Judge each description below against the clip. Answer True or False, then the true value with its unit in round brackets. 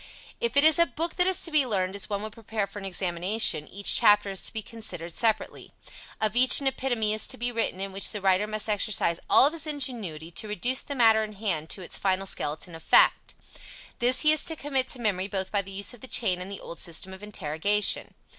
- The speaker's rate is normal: False (240 wpm)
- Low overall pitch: False (210 Hz)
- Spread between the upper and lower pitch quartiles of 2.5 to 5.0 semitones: True (4.4 semitones)